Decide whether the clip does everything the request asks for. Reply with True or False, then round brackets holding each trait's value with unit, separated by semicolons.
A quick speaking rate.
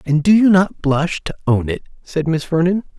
True (220 wpm)